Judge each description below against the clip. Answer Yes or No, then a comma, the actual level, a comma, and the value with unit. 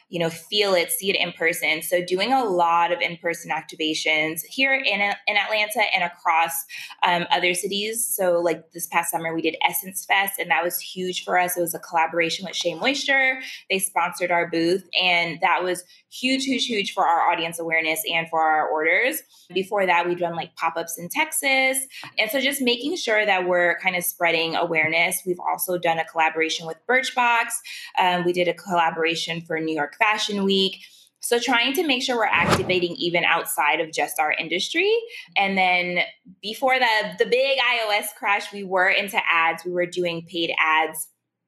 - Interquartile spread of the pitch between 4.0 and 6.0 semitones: Yes, average, 4.3 semitones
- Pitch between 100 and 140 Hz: No, medium, 180 Hz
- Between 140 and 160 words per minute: No, average, 190 wpm